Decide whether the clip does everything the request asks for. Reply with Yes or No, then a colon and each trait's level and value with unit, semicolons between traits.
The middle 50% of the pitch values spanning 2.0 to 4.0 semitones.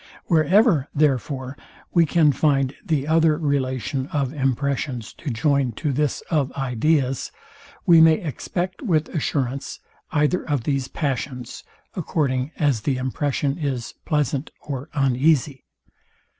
Yes: average, 3.0 semitones